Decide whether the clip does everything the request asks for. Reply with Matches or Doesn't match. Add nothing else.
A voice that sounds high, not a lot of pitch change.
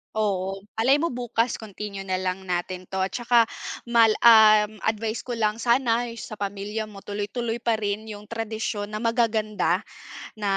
Matches